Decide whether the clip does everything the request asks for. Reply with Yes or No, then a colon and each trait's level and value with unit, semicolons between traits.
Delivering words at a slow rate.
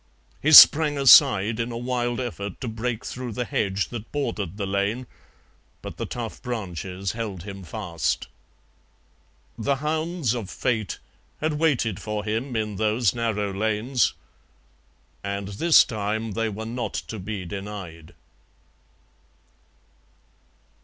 Yes: slow, 125 wpm